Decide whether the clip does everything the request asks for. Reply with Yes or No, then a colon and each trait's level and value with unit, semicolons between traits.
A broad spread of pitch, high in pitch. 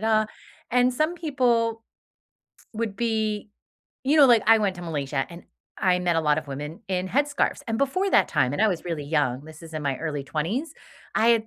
Yes: wide, 7.1 semitones; high, 205 Hz